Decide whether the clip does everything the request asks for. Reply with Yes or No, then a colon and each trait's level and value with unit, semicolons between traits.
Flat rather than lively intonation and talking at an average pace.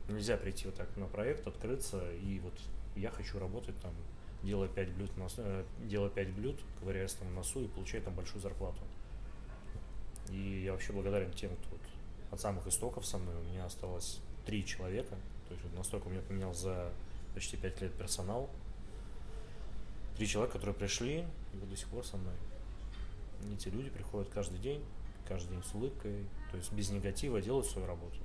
No: narrow, 1.8 semitones; fast, 185 wpm